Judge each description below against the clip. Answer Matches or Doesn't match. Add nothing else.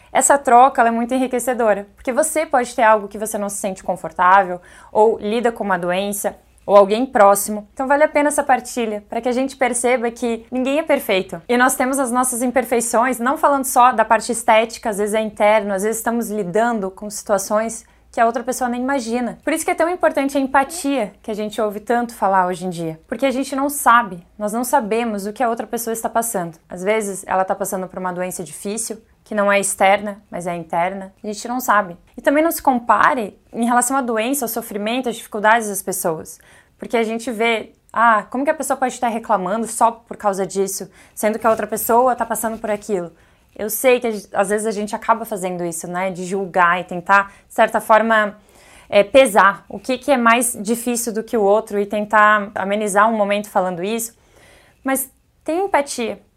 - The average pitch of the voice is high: Matches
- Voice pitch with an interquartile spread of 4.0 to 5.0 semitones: Doesn't match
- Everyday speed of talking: Doesn't match